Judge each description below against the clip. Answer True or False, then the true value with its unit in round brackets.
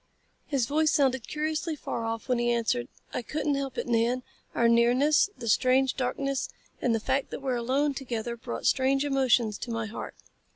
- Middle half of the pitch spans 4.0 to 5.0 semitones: False (2.8 semitones)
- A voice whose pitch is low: False (255 Hz)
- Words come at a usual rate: True (190 wpm)